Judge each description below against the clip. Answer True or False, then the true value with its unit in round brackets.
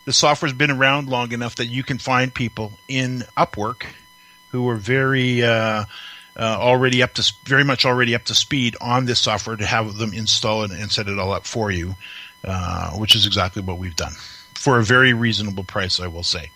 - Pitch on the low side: True (115 Hz)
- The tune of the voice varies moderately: True (3.4 semitones)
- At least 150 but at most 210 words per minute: True (205 wpm)